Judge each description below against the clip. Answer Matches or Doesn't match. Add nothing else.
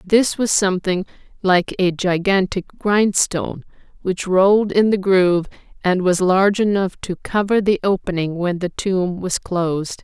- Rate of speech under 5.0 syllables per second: Matches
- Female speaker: Matches